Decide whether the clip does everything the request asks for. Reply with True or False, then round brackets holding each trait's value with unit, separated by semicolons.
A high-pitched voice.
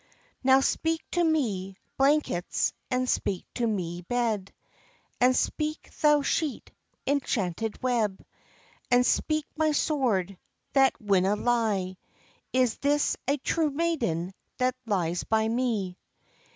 True (245 Hz)